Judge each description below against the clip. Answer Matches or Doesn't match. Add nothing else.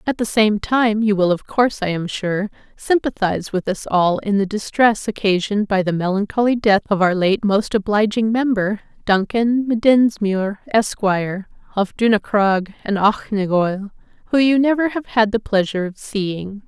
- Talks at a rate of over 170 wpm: Doesn't match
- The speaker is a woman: Matches